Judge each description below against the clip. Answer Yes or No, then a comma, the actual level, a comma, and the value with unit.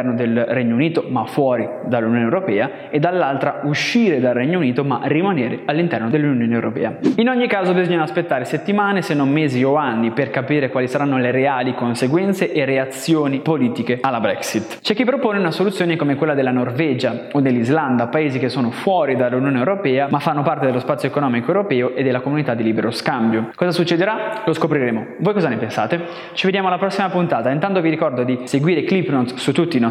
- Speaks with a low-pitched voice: No, medium, 145 Hz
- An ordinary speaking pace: No, fast, 190 wpm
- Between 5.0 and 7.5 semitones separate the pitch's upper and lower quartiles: Yes, wide, 5.5 semitones